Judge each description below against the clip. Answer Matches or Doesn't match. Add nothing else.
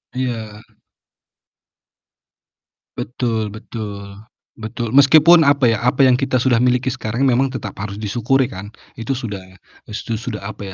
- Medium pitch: Doesn't match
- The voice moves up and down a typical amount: Matches